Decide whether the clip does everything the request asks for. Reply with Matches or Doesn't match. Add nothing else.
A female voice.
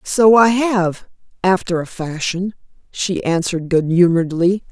Matches